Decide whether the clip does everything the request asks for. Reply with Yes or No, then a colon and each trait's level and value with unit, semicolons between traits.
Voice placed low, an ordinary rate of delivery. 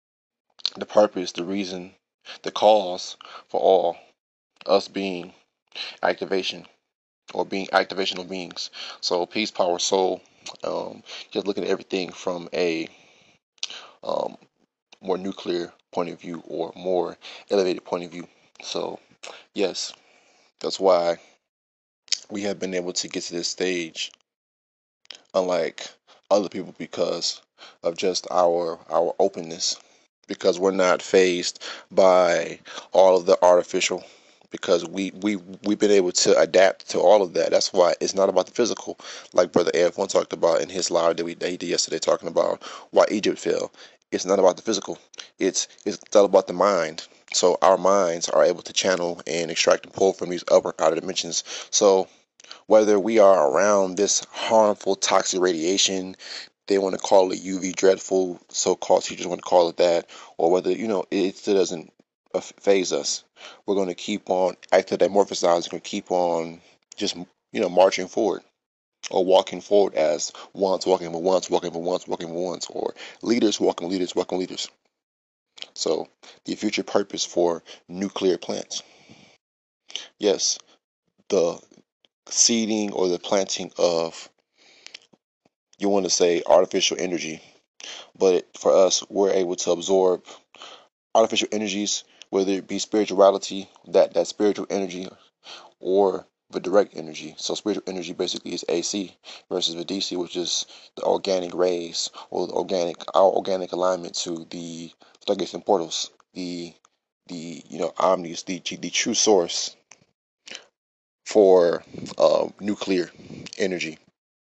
Yes: very low, 90 Hz; average, 150 wpm